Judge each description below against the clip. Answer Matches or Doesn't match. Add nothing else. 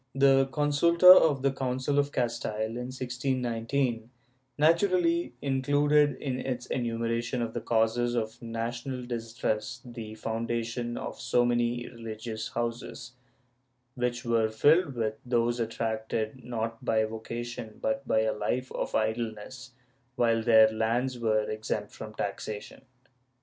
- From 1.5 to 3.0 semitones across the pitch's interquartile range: Matches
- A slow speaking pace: Matches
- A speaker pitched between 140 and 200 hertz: Doesn't match